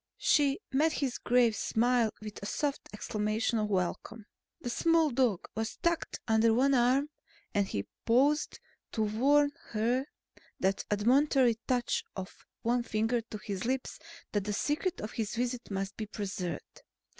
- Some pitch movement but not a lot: Yes, average, 4.0 semitones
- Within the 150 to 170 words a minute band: Yes, average, 155 wpm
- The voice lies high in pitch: Yes, high, 235 Hz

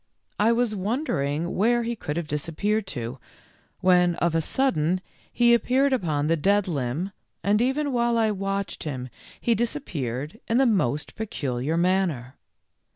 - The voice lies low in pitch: No, high, 190 Hz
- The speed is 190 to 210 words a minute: No, average, 155 wpm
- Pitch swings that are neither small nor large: No, wide, 7.5 semitones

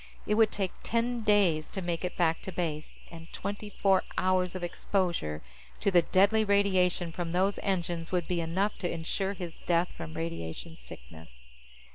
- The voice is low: No, medium, 180 Hz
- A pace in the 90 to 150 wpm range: No, average, 170 wpm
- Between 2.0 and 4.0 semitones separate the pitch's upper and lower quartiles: Yes, average, 3.1 semitones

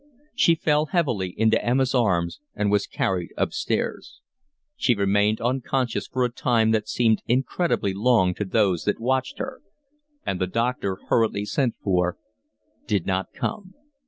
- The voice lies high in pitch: No, low, 110 Hz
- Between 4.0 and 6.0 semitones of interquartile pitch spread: Yes, average, 4.7 semitones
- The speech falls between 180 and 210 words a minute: No, average, 145 wpm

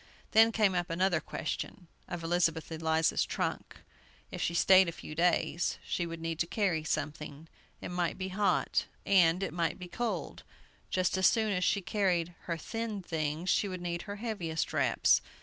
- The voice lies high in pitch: No, medium, 175 Hz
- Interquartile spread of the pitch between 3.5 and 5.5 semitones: No, average, 2.8 semitones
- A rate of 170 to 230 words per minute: Yes, average, 175 wpm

